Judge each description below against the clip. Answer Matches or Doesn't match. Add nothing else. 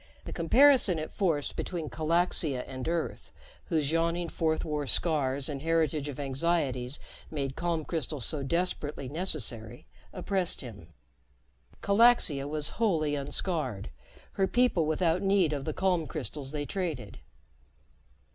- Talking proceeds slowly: Matches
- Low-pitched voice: Doesn't match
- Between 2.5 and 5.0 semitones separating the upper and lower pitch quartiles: Matches